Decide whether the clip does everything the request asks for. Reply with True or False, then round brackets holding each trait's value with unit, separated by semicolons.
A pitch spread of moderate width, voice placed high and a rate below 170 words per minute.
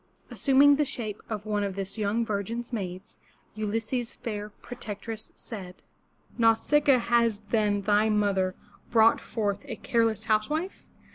False (2.3 semitones; 220 Hz; 140 wpm)